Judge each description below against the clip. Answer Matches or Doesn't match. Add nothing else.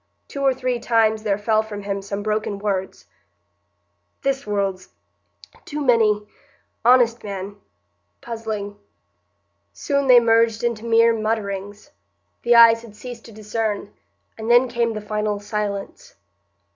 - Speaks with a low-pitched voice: Doesn't match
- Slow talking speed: Matches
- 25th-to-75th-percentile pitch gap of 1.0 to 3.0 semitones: Matches